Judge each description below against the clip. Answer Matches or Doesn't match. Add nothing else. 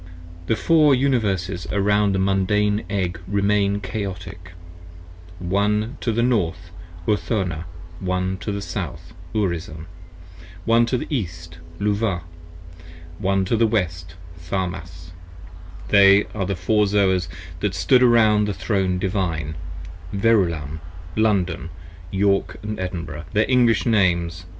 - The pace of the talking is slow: Matches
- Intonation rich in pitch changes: Doesn't match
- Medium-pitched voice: Doesn't match